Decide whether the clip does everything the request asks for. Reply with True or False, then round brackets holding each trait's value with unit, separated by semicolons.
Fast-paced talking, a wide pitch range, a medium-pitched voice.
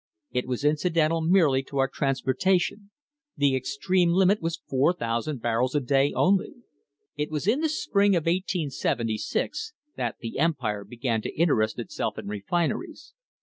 False (145 wpm; 5.9 semitones; 150 Hz)